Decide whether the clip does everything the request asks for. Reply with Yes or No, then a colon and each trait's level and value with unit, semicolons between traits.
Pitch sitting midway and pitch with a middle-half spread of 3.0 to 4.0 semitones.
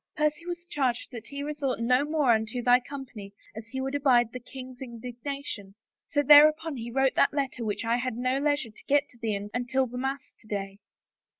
No: very high, 255 Hz; average, 3.3 semitones